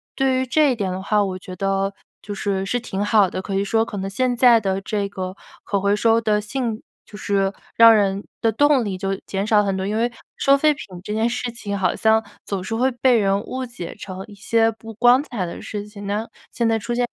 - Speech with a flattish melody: No, average, 3.1 semitones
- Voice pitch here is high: Yes, high, 210 Hz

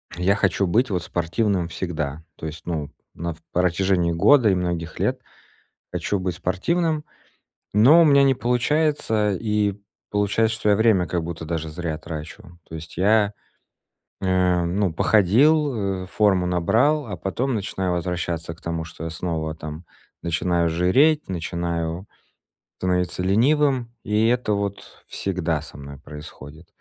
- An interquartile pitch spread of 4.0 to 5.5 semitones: Yes, average, 4.4 semitones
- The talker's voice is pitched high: No, very low, 90 Hz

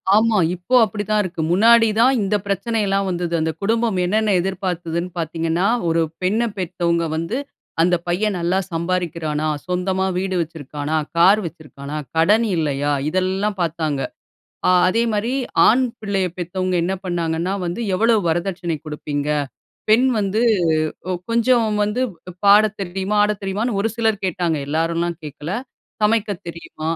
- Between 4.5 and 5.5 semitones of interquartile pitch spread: No, average, 4.0 semitones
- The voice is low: No, medium, 185 Hz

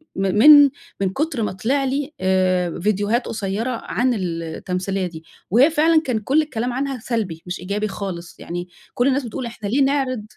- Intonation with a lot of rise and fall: Yes, wide, 6.0 semitones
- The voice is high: Yes, high, 220 Hz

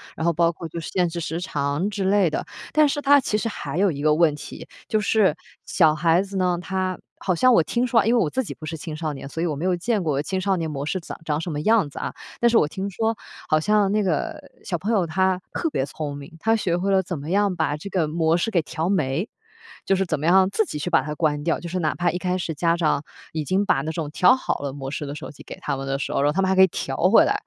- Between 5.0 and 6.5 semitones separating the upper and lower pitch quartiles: No, average, 4.2 semitones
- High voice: No, medium, 175 Hz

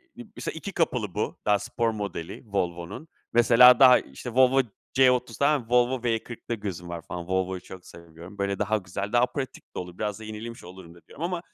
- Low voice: Yes, low, 110 Hz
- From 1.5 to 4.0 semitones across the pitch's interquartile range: No, average, 5.2 semitones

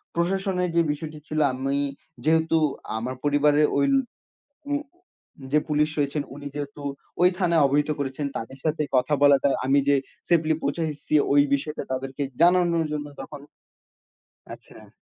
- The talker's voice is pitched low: No, medium, 150 Hz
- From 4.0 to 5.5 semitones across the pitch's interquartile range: No, narrow, 2.4 semitones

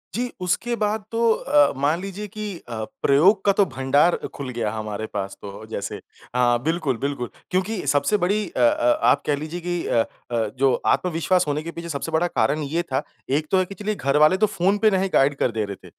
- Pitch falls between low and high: Yes, medium, 155 Hz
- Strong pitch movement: Yes, wide, 6.7 semitones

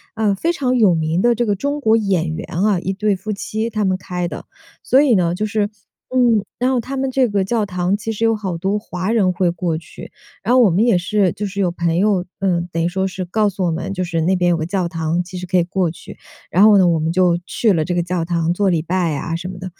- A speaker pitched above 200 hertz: No, medium, 185 Hz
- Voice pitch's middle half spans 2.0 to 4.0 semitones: Yes, average, 3.5 semitones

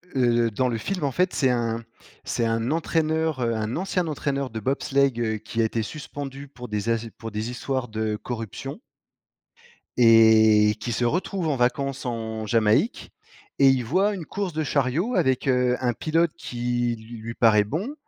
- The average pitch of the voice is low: Yes, low, 125 Hz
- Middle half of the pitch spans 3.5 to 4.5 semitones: Yes, average, 4.2 semitones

